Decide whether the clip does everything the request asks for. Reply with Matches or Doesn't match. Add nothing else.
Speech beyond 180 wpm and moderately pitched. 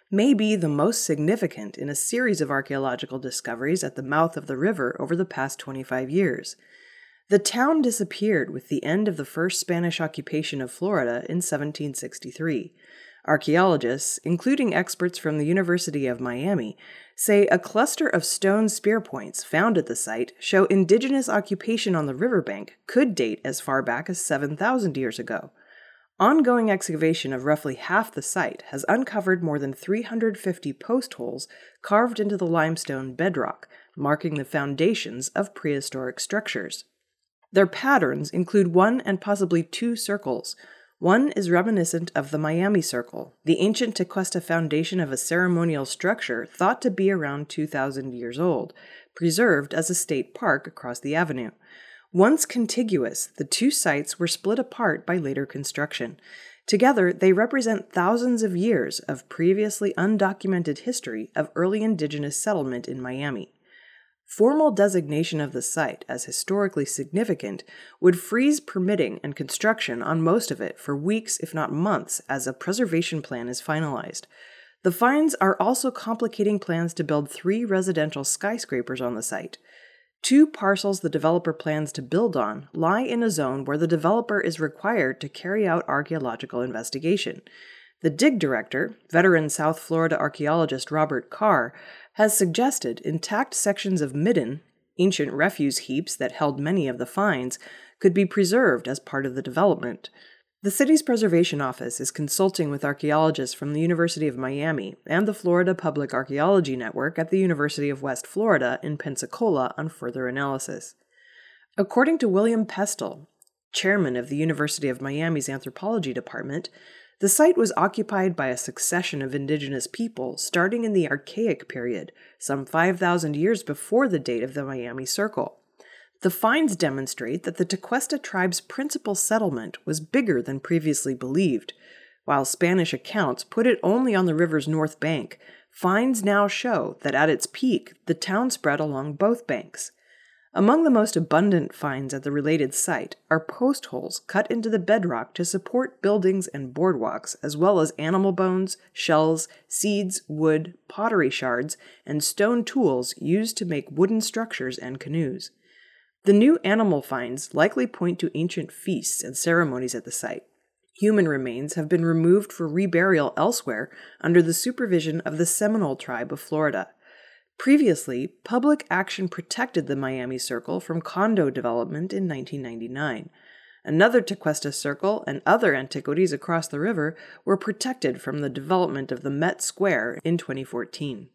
Doesn't match